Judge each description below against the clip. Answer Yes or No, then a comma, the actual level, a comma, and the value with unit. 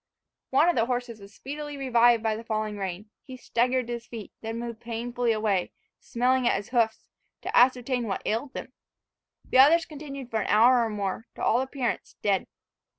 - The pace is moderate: Yes, average, 190 wpm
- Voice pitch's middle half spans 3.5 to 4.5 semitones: No, narrow, 2.6 semitones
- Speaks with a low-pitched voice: No, high, 235 Hz